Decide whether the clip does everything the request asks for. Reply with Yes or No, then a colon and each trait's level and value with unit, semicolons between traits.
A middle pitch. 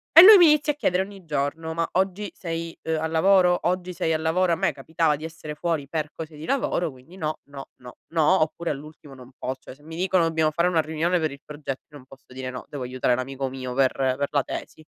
Yes: medium, 160 Hz